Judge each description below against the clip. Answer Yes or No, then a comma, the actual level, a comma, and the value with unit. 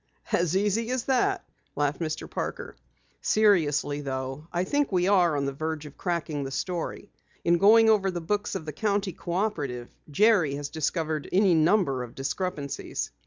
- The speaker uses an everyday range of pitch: No, wide, 5.7 semitones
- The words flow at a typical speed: Yes, average, 165 wpm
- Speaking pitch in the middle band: Yes, medium, 170 Hz